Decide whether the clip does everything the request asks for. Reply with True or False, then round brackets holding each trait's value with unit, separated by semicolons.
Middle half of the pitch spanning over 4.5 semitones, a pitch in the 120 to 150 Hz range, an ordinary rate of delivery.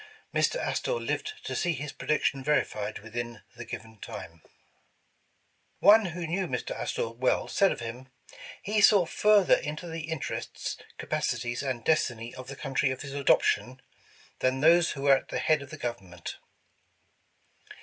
True (5.3 semitones; 135 Hz; 160 wpm)